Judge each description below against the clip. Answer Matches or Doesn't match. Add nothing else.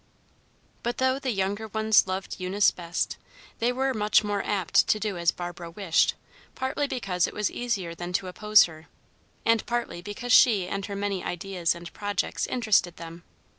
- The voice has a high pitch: Matches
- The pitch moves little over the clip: Doesn't match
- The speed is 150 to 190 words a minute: Matches